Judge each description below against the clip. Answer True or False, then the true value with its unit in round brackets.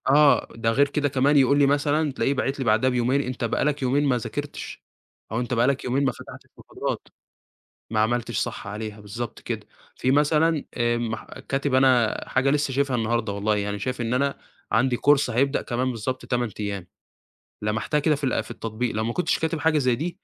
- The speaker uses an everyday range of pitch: True (3.6 semitones)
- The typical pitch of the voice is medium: False (130 Hz)